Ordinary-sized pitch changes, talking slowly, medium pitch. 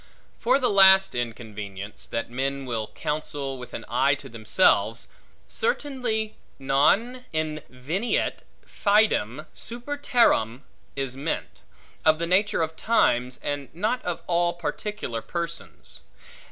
No: wide, 8.6 semitones; slow, 115 wpm; medium, 155 Hz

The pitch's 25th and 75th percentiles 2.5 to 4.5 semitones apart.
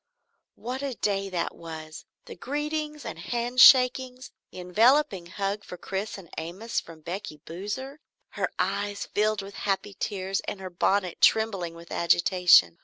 No: average, 5.3 semitones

